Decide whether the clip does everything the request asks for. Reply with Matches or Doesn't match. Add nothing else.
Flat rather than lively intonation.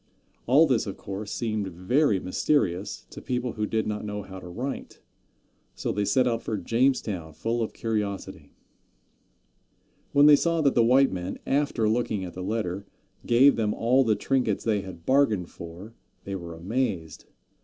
Doesn't match